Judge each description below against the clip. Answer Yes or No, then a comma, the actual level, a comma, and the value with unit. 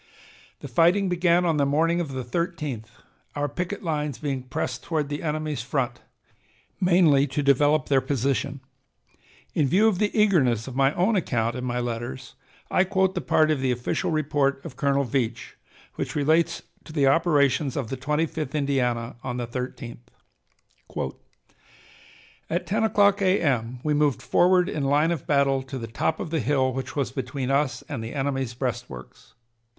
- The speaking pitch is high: No, medium, 140 Hz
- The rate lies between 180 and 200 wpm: No, average, 170 wpm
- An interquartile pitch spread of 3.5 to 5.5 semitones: Yes, average, 4.0 semitones